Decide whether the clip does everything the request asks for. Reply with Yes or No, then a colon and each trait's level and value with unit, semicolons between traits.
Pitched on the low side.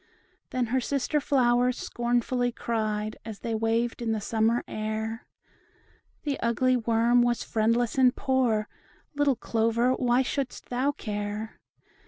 No: high, 235 Hz